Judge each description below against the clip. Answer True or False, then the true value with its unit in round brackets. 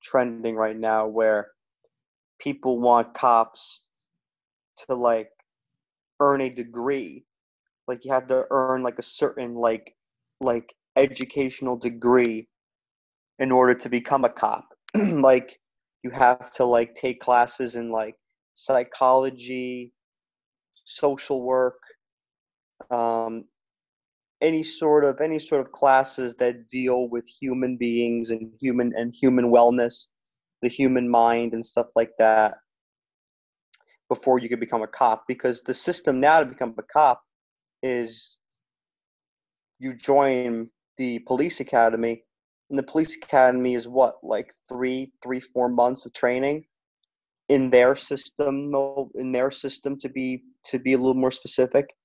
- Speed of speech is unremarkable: False (130 wpm)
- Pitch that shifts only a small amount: True (1.9 semitones)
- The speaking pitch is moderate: False (125 Hz)